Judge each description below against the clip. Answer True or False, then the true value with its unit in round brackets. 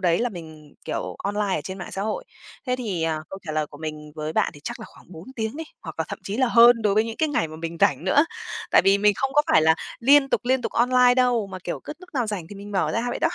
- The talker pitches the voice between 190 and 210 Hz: True (205 Hz)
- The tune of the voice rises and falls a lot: True (6.9 semitones)